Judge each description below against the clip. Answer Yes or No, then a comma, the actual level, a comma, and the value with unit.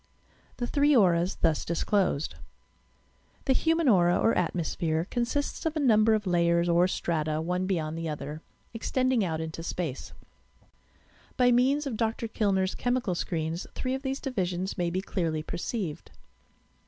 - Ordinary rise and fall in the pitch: No, wide, 6.3 semitones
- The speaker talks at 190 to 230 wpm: No, average, 145 wpm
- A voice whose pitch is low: No, medium, 185 Hz